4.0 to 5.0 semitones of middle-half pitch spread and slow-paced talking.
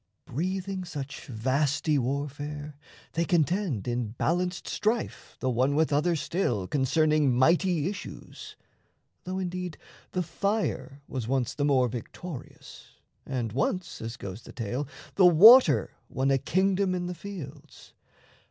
No: wide, 5.6 semitones; slow, 130 wpm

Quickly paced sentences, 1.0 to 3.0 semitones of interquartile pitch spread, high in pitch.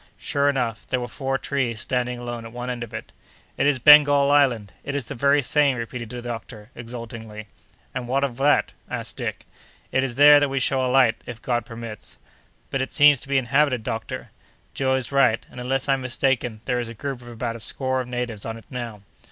No: fast, 215 wpm; narrow, 2.6 semitones; low, 125 Hz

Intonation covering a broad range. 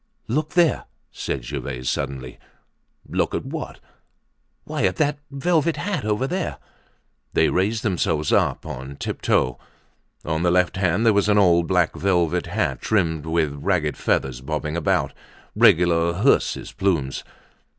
Yes: wide, 5.9 semitones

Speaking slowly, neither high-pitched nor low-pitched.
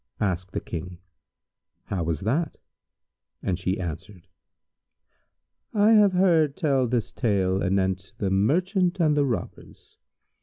No: slow, 120 wpm; low, 105 Hz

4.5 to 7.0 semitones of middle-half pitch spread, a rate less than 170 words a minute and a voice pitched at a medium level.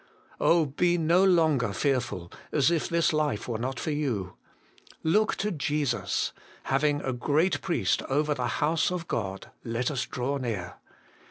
Yes: average, 4.8 semitones; average, 155 wpm; medium, 145 Hz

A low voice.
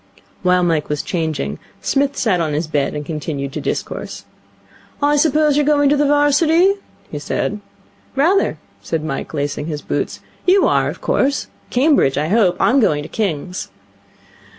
No: medium, 185 Hz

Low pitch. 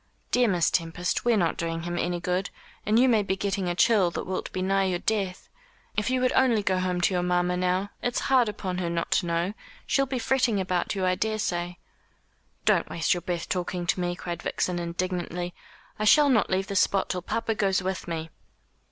No: medium, 185 Hz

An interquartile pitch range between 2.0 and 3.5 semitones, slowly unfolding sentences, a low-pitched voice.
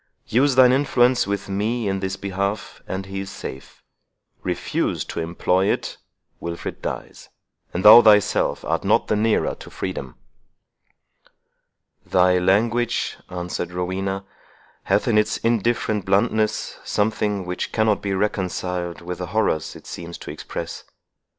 Yes: average, 3.1 semitones; slow, 130 wpm; low, 100 Hz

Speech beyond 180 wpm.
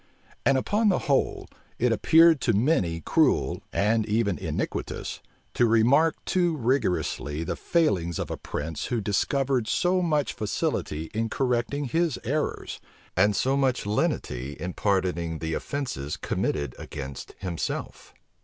No: slow, 135 wpm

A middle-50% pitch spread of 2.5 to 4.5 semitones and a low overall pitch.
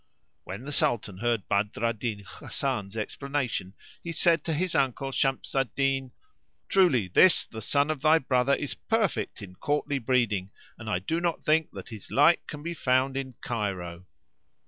No: wide, 5.4 semitones; low, 130 Hz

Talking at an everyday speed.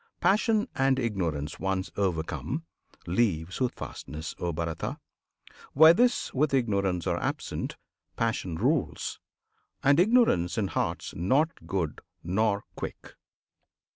No: slow, 105 wpm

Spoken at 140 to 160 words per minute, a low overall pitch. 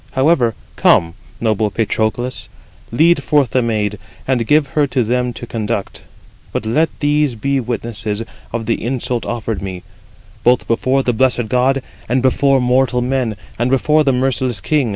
Yes: average, 155 wpm; low, 125 Hz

